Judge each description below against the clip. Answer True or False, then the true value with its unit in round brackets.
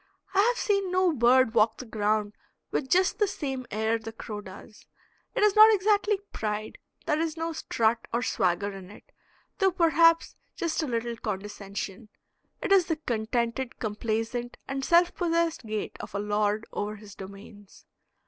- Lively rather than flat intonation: True (7.8 semitones)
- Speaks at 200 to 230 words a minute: False (165 wpm)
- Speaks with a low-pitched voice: False (235 Hz)